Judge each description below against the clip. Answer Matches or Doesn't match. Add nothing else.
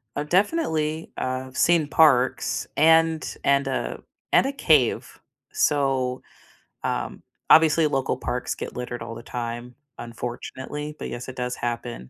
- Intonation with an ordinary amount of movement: Matches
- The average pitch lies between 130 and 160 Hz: Matches